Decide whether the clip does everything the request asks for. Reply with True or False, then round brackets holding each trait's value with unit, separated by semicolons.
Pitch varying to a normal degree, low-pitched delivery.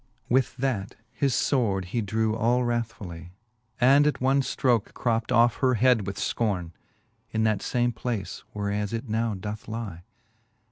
True (3.2 semitones; 115 Hz)